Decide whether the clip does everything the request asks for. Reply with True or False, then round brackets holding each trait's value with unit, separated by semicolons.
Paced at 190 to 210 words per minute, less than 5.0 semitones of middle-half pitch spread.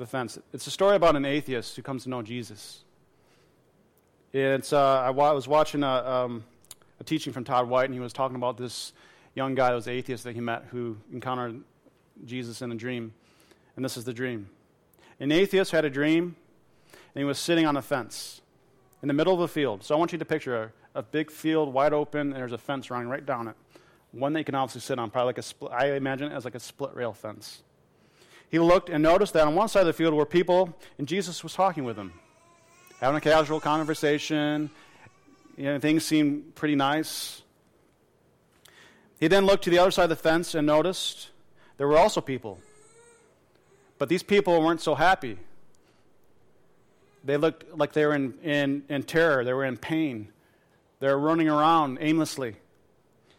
True (200 wpm; 3.9 semitones)